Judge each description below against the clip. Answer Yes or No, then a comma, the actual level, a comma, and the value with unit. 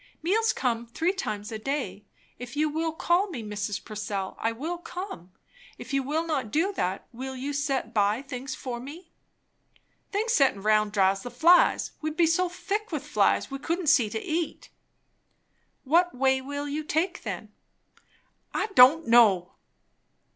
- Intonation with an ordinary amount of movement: No, wide, 6.6 semitones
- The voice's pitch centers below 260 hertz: No, very high, 275 Hz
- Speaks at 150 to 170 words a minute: Yes, average, 160 wpm